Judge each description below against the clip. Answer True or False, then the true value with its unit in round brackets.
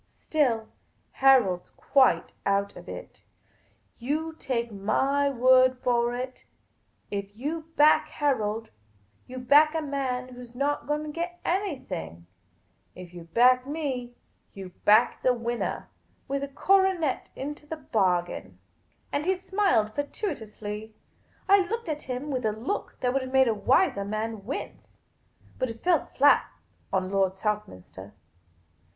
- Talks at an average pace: True (145 wpm)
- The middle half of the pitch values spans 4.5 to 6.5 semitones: True (5.4 semitones)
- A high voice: True (255 Hz)